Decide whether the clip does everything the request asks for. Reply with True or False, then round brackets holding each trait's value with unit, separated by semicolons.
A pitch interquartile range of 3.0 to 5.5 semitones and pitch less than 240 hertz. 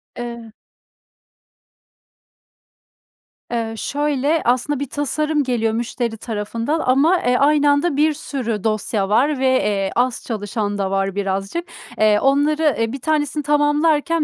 False (4.9 semitones; 260 Hz)